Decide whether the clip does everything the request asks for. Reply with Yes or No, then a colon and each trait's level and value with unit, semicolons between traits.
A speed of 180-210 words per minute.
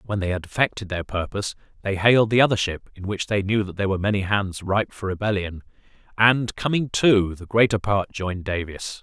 Yes: fast, 205 wpm